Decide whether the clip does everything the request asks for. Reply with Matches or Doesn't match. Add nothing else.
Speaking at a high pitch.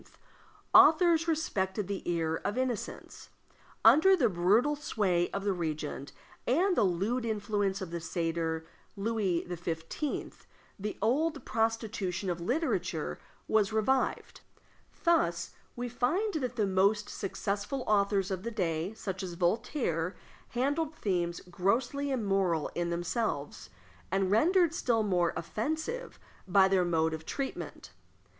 Matches